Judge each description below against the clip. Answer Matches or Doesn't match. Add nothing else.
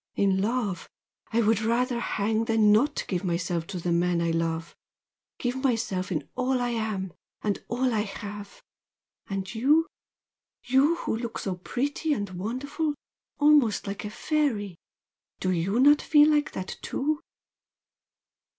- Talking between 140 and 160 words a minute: Matches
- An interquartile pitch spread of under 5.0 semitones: Doesn't match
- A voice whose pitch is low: Doesn't match